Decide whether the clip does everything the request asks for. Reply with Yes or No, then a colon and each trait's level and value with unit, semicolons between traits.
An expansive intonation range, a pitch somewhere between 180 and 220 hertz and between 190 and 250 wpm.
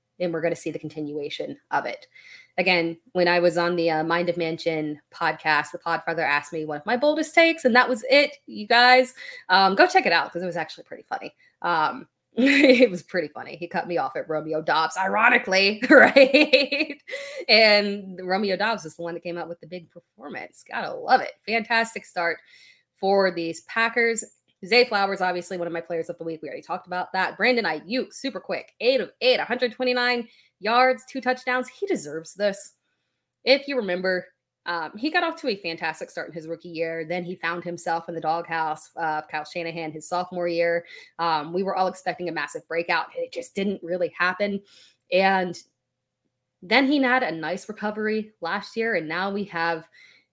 Yes: wide, 6.7 semitones; medium, 185 Hz; average, 200 wpm